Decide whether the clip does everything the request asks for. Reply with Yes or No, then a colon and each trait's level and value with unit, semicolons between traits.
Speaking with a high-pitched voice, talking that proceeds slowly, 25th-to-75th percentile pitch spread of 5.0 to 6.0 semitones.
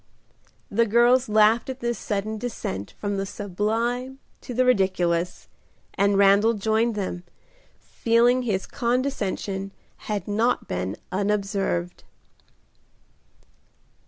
No: high, 210 Hz; slow, 100 wpm; average, 3.3 semitones